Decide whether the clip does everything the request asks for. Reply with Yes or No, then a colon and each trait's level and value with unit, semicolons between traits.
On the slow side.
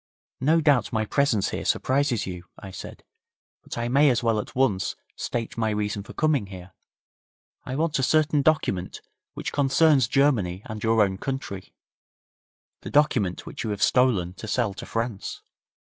No: average, 165 wpm